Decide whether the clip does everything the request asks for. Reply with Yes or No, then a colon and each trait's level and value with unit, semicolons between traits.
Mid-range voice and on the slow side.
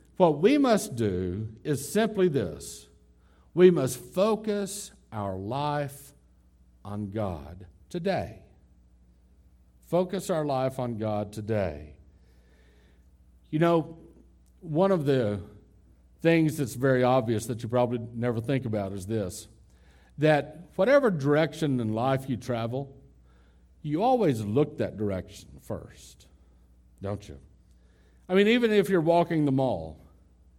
No: low, 110 Hz; slow, 120 wpm